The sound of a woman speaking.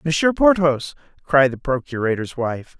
No: male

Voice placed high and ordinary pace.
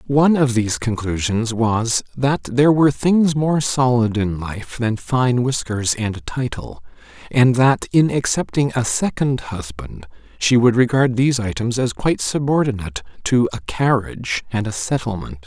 No: low, 120 Hz; average, 155 wpm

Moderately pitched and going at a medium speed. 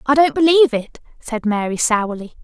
No: very high, 250 Hz; average, 170 wpm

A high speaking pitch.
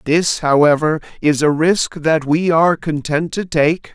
No: medium, 155 Hz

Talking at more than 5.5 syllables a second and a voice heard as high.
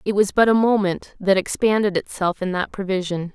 No: 5.3 syllables/s; high, 195 Hz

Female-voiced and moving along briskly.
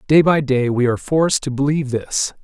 No: male; fast, 220 wpm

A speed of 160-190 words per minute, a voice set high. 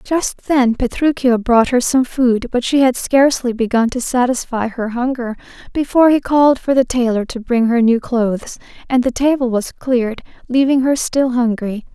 Yes: average, 175 wpm; very high, 250 Hz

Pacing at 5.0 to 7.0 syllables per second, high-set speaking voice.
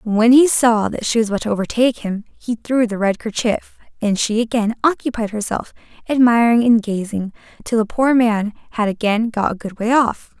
Yes: 5.3 syllables/s; high, 225 Hz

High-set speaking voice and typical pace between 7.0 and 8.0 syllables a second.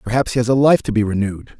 No: low, 115 Hz; 7.4 syllables/s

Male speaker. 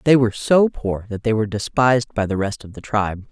No: female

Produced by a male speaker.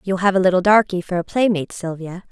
No: female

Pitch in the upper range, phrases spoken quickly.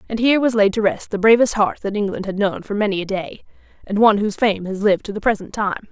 Yes: high, 205 Hz; fast, 275 wpm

